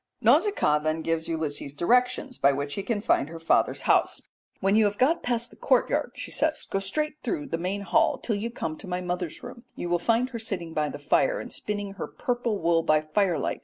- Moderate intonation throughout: No, wide, 6.4 semitones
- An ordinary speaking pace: No, fast, 220 wpm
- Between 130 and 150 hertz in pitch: No, high, 195 Hz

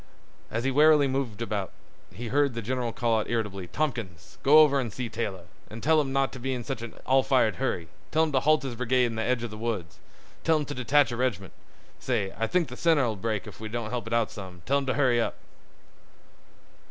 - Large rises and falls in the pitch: No, average, 3.5 semitones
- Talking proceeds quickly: Yes, fast, 235 wpm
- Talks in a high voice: No, low, 120 Hz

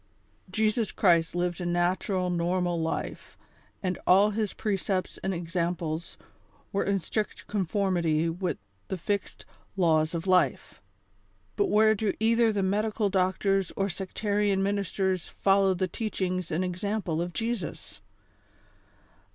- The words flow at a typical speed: No, slow, 130 wpm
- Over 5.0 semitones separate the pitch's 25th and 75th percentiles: No, narrow, 2.6 semitones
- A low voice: No, high, 190 Hz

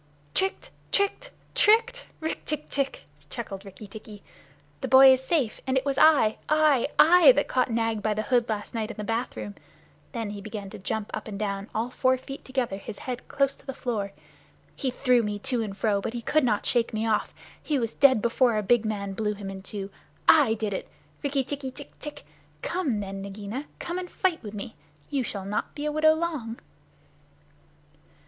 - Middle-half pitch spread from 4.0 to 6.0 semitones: Yes, average, 5.0 semitones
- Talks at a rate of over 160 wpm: Yes, average, 200 wpm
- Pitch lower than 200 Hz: No, high, 235 Hz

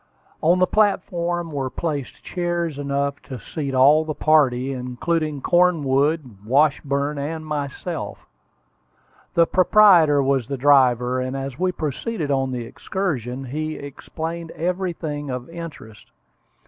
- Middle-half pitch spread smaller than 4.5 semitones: Yes, average, 3.9 semitones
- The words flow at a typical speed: No, slow, 120 wpm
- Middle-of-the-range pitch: Yes, medium, 145 Hz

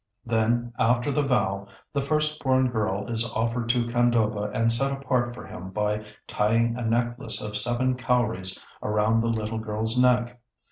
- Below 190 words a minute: Yes, average, 160 wpm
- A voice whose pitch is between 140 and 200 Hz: No, low, 115 Hz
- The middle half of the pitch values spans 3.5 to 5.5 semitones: No, narrow, 2.4 semitones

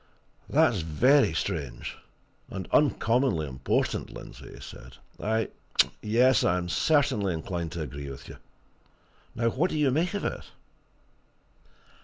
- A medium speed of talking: No, slow, 130 wpm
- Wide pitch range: Yes, wide, 8.2 semitones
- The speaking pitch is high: No, low, 105 Hz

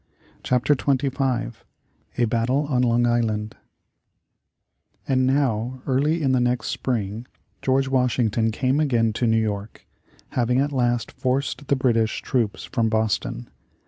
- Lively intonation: No, average, 2.9 semitones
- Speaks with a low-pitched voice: Yes, low, 125 Hz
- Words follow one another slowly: Yes, slow, 130 wpm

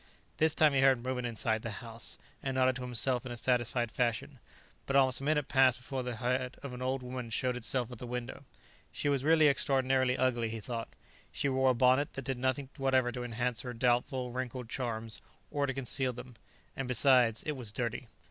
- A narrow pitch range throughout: Yes, narrow, 1.7 semitones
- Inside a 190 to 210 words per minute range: Yes, fast, 205 wpm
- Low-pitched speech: Yes, low, 125 Hz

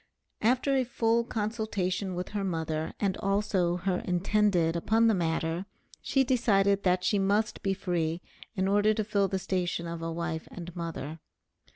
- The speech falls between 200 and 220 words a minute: No, average, 165 wpm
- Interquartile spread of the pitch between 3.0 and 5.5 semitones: Yes, average, 3.6 semitones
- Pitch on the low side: No, high, 195 Hz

